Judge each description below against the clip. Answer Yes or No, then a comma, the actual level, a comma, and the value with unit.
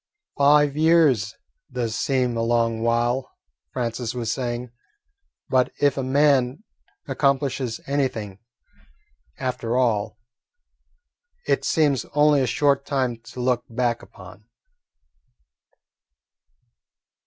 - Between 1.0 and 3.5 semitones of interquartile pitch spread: Yes, average, 3.0 semitones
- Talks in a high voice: No, low, 125 Hz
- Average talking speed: No, slow, 95 wpm